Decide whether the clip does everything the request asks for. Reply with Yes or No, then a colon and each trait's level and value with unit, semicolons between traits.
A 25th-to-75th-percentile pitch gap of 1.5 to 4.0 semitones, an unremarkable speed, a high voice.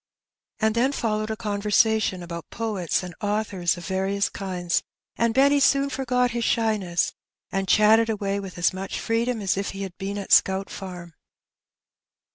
Yes: average, 3.1 semitones; average, 165 wpm; high, 205 Hz